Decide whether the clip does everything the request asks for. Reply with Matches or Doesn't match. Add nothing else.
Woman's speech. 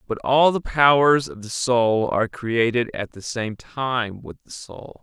Doesn't match